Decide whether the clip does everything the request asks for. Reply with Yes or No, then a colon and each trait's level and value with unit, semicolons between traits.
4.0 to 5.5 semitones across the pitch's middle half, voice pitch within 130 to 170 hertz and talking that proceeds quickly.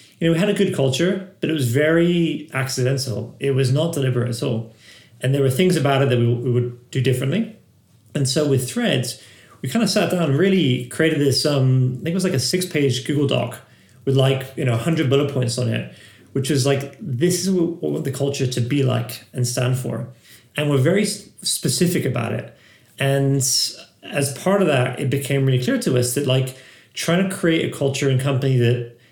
Yes: average, 4.3 semitones; low, 135 Hz; fast, 220 wpm